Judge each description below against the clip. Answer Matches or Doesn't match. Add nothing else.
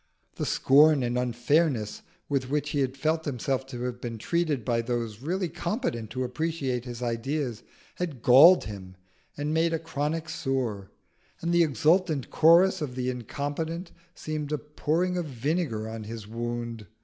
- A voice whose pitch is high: Doesn't match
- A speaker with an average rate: Matches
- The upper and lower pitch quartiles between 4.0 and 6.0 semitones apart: Matches